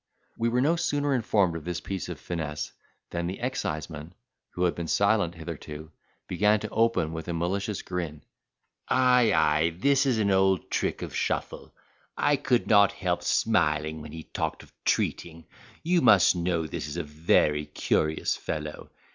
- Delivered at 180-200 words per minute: No, average, 165 wpm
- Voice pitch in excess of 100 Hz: No, very low, 90 Hz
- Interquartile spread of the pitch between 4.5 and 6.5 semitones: Yes, wide, 5.5 semitones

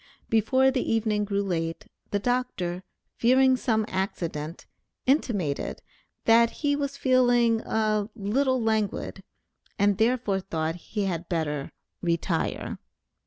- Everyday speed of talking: No, slow, 120 wpm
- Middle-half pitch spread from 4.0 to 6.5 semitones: Yes, average, 5.3 semitones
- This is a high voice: Yes, high, 215 Hz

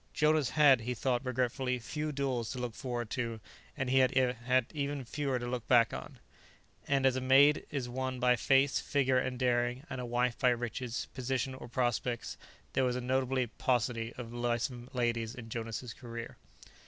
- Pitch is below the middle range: Yes, low, 125 Hz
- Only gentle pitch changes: Yes, narrow, 1.7 semitones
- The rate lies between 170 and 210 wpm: Yes, average, 180 wpm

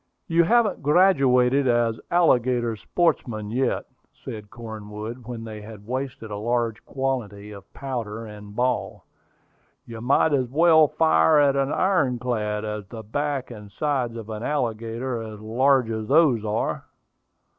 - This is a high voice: No, low, 120 Hz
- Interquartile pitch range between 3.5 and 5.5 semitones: Yes, average, 4.0 semitones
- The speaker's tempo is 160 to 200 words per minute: No, average, 145 wpm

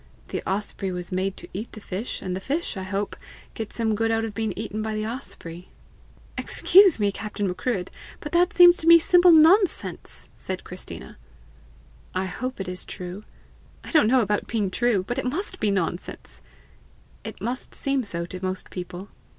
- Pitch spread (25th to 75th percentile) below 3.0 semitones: No, wide, 5.5 semitones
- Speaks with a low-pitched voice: No, high, 215 Hz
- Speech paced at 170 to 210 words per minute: Yes, average, 180 wpm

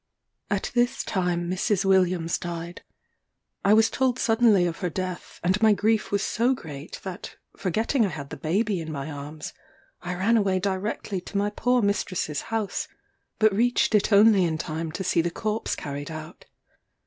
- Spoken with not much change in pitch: No, average, 4.2 semitones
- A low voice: No, high, 190 Hz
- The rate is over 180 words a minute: No, average, 170 wpm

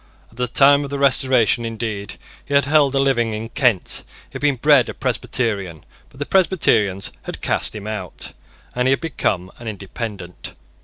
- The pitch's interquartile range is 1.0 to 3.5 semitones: No, average, 4.6 semitones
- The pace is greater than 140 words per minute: Yes, average, 185 wpm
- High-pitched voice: No, low, 120 Hz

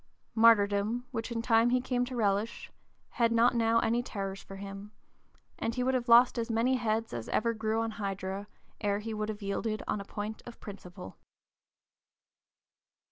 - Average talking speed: Yes, average, 175 wpm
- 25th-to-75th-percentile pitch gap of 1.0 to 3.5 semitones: Yes, narrow, 2.5 semitones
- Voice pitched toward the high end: Yes, high, 225 Hz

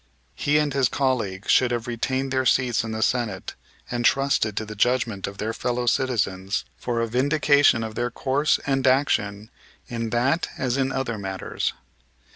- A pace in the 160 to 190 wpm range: Yes, average, 170 wpm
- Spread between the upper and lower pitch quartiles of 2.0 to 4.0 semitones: Yes, average, 3.3 semitones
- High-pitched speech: No, low, 120 Hz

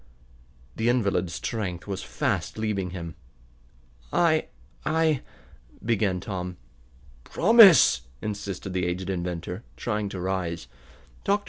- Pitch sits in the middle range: No, very low, 95 Hz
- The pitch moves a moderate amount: Yes, average, 4.3 semitones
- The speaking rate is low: Yes, slow, 110 wpm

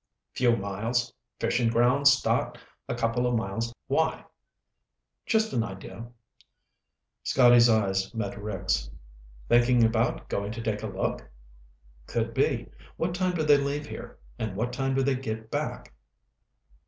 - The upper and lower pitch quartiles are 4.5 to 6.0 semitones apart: No, average, 3.6 semitones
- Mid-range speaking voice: No, low, 120 Hz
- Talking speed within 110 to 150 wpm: Yes, average, 140 wpm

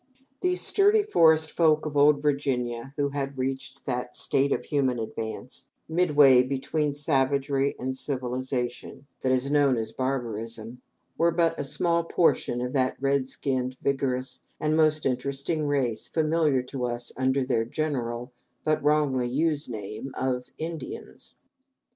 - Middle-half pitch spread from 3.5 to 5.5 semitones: No, average, 3.1 semitones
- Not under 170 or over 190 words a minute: No, average, 140 wpm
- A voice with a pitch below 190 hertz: Yes, low, 135 Hz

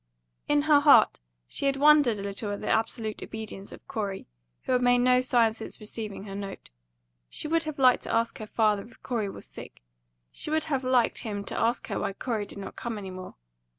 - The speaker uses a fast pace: Yes, fast, 220 wpm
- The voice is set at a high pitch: Yes, high, 230 Hz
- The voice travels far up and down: No, average, 3.9 semitones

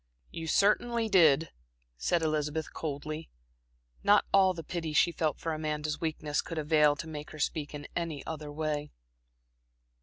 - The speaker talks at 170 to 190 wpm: No, average, 150 wpm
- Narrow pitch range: Yes, narrow, 1.7 semitones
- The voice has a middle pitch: Yes, medium, 155 Hz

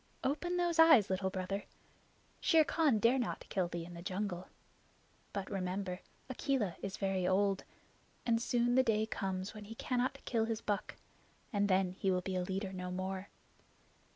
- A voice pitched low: No, high, 200 Hz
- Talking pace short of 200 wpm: Yes, average, 165 wpm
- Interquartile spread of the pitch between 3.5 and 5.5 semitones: Yes, average, 4.1 semitones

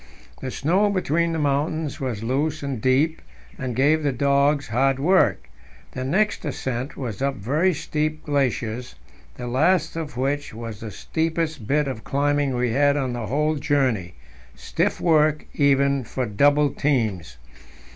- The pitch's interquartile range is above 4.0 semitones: No, average, 3.3 semitones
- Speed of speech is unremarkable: Yes, average, 150 wpm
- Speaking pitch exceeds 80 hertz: Yes, medium, 140 Hz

